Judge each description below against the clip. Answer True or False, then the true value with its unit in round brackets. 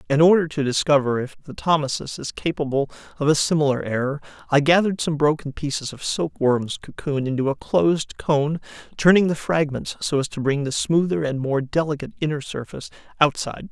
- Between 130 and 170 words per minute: False (180 wpm)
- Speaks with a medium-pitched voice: True (145 Hz)